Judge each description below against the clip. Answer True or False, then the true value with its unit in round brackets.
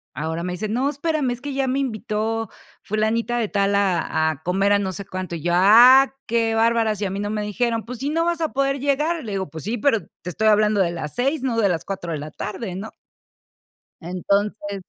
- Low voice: False (215 Hz)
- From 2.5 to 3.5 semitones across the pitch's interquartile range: False (4.3 semitones)